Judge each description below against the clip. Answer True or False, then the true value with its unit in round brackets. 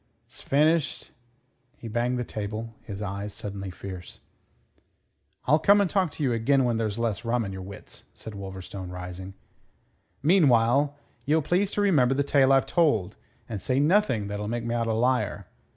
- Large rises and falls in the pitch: True (5.7 semitones)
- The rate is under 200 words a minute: True (170 wpm)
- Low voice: True (115 Hz)